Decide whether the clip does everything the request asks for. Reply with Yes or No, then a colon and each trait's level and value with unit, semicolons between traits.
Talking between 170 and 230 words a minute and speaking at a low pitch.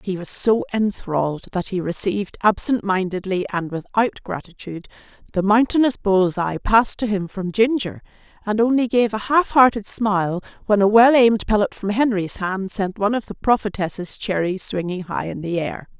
No: average, 175 wpm; high, 200 Hz